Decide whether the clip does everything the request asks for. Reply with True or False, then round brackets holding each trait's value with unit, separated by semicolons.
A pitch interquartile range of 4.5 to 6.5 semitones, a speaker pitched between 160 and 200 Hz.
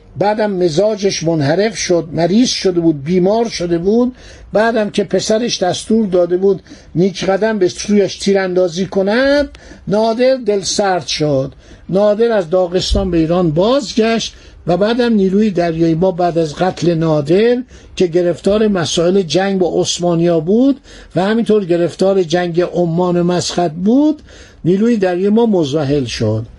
False (3.4 semitones; 185 Hz)